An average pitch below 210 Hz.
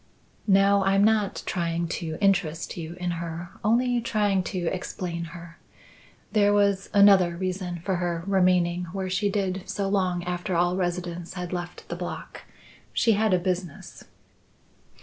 Yes: medium, 185 Hz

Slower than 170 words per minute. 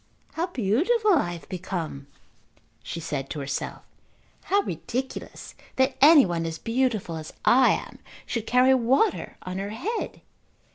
Yes: average, 140 wpm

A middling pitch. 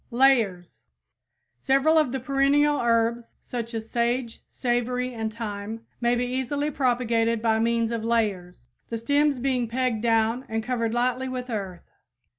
No: high, 235 Hz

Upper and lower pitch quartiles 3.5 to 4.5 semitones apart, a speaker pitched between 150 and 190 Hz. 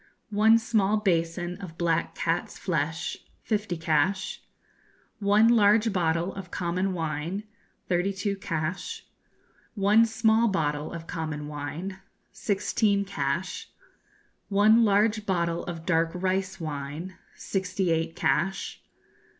Yes: average, 3.8 semitones; medium, 185 Hz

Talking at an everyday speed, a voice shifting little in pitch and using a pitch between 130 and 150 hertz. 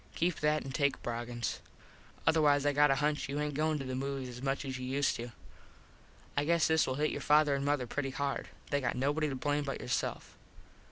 No: fast, 220 wpm; narrow, 2.0 semitones; medium, 140 Hz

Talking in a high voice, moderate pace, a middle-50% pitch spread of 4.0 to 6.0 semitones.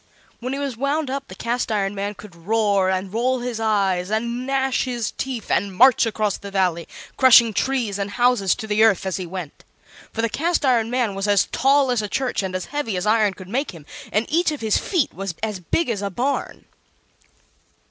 No: high, 220 Hz; fast, 215 wpm; average, 4.6 semitones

